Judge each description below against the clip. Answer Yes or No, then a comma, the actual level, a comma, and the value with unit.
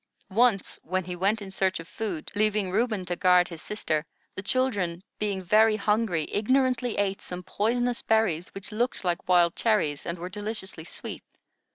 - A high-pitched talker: Yes, high, 195 Hz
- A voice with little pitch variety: No, average, 3.6 semitones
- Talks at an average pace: Yes, average, 170 wpm